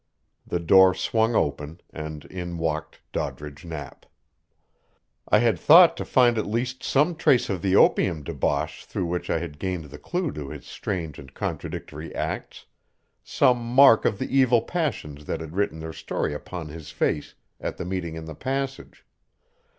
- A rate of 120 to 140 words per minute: No, average, 165 wpm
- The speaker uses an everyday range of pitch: No, wide, 7.2 semitones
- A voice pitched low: Yes, very low, 90 Hz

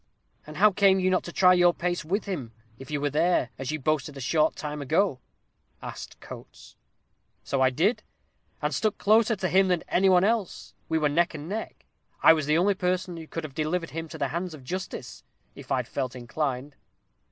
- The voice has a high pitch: No, medium, 165 Hz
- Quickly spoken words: Yes, fast, 210 wpm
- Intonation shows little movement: No, average, 4.2 semitones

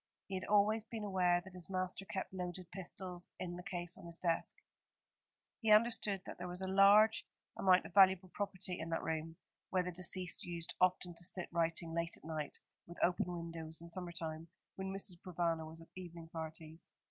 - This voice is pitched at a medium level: Yes, medium, 180 Hz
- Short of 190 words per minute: No, average, 195 wpm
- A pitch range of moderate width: No, narrow, 2.2 semitones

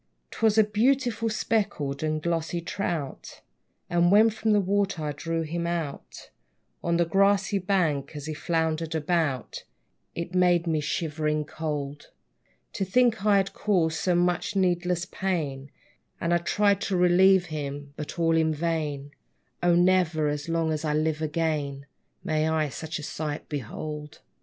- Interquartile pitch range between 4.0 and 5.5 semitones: No, average, 3.5 semitones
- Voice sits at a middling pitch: Yes, medium, 165 Hz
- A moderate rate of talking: Yes, average, 150 wpm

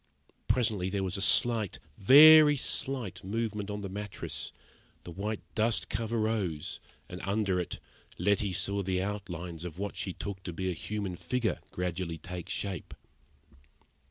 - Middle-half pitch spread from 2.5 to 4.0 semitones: Yes, average, 3.1 semitones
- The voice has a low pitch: Yes, low, 100 Hz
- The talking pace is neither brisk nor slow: Yes, average, 150 wpm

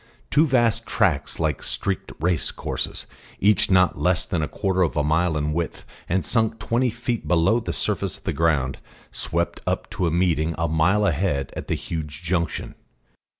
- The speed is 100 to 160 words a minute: No, average, 180 wpm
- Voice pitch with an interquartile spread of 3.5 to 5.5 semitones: Yes, average, 3.9 semitones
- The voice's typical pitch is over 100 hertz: No, very low, 85 Hz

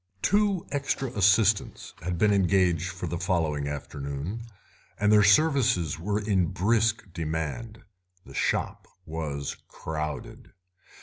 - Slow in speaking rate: Yes, slow, 115 wpm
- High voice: No, very low, 95 Hz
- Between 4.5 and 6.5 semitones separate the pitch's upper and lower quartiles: Yes, average, 5.3 semitones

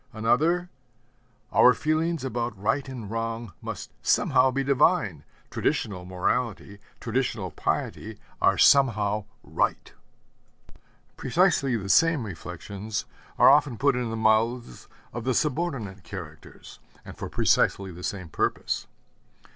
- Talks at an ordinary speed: No, slow, 115 wpm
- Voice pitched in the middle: No, low, 115 Hz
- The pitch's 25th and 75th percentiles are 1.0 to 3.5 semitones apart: No, average, 5.0 semitones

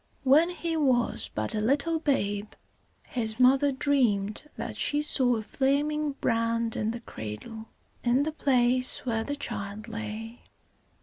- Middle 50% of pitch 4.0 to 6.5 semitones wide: Yes, average, 4.3 semitones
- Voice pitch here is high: Yes, high, 245 Hz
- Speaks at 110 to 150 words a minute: Yes, average, 140 wpm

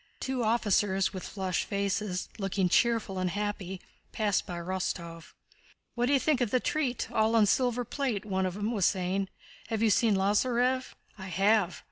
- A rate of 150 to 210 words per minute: Yes, average, 165 wpm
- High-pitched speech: Yes, high, 205 Hz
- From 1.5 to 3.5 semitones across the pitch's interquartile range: No, average, 3.9 semitones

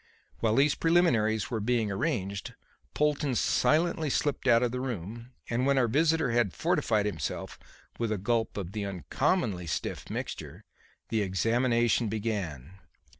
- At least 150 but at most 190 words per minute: No, average, 140 wpm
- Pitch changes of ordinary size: Yes, average, 4.8 semitones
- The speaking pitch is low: Yes, low, 115 Hz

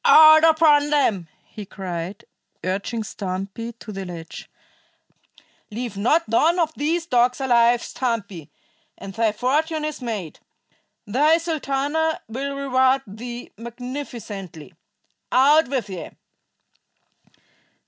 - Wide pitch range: Yes, wide, 6.2 semitones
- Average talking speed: No, slow, 105 wpm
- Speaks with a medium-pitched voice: No, high, 245 Hz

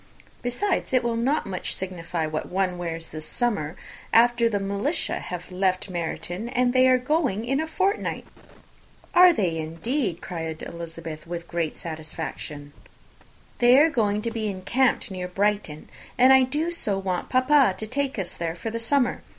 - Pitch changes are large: Yes, wide, 6.9 semitones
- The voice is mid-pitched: No, high, 205 Hz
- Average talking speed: Yes, average, 170 wpm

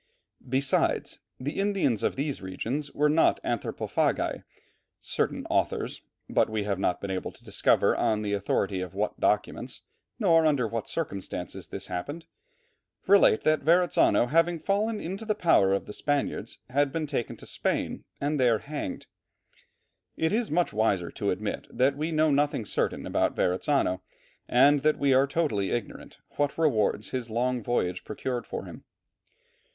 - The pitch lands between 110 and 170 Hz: Yes, low, 135 Hz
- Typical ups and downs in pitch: No, wide, 6.6 semitones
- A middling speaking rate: Yes, average, 155 wpm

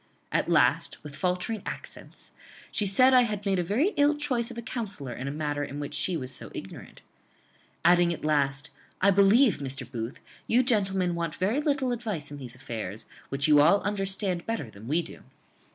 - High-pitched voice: No, medium, 180 Hz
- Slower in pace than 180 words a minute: No, average, 190 wpm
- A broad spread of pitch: Yes, wide, 7.5 semitones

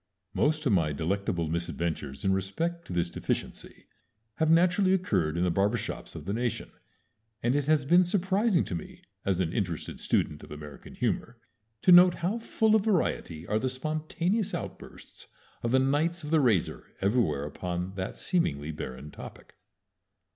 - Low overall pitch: Yes, low, 115 Hz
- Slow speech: No, average, 165 wpm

